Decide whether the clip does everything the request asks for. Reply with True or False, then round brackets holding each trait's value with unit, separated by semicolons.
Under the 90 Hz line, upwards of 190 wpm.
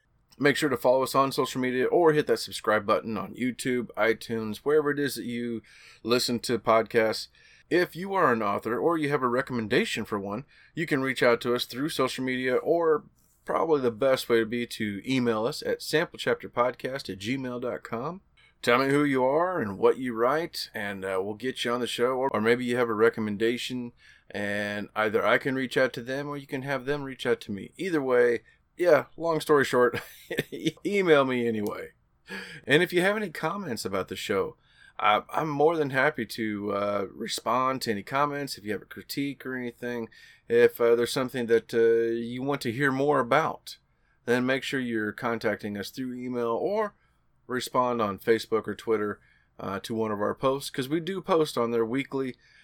False (125 Hz; 200 wpm)